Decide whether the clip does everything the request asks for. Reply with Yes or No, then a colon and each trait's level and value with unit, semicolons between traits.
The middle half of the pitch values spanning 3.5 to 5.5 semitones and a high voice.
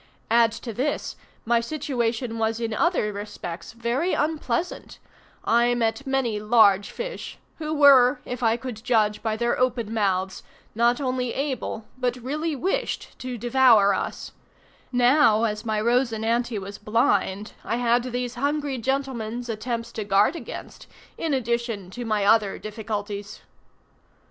No: average, 2.9 semitones; high, 235 Hz